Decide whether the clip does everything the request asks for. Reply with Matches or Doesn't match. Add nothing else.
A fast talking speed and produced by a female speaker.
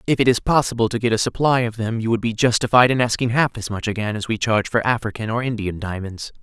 Doesn't match